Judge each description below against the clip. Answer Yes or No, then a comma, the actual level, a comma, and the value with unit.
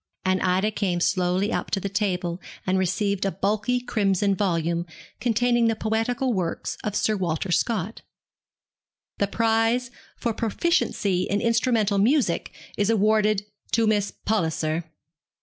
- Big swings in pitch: No, average, 3.3 semitones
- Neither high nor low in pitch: No, high, 205 Hz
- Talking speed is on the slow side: Yes, slow, 130 wpm